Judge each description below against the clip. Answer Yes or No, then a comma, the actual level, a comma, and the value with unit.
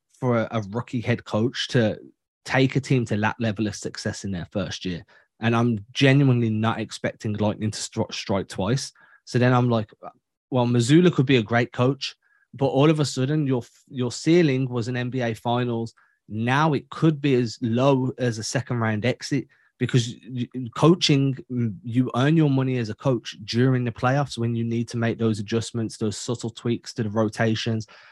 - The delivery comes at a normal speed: Yes, average, 185 wpm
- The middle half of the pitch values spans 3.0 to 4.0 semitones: No, narrow, 2.6 semitones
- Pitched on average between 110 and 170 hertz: Yes, low, 120 Hz